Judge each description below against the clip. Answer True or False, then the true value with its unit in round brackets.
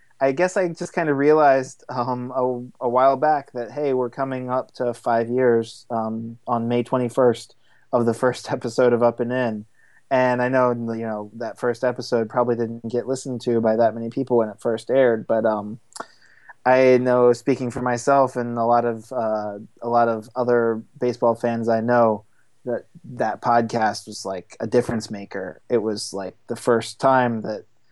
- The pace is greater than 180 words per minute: True (190 wpm)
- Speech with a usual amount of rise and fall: False (1.8 semitones)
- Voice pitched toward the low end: True (120 Hz)